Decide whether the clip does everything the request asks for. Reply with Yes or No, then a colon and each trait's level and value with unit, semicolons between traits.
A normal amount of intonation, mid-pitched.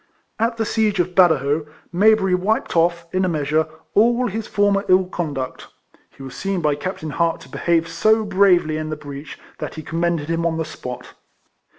Yes: average, 4.1 semitones; medium, 170 Hz